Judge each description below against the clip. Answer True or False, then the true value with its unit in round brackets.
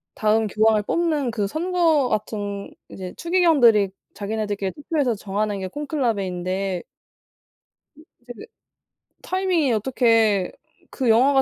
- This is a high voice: True (225 Hz)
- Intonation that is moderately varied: False (6.1 semitones)